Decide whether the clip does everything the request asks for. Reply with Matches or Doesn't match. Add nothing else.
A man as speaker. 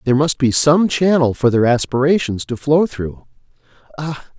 Matches